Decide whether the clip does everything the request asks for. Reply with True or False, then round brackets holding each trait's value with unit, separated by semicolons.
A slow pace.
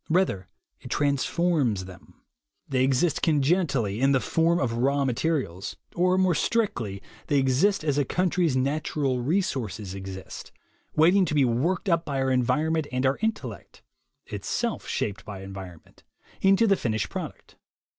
False (145 wpm)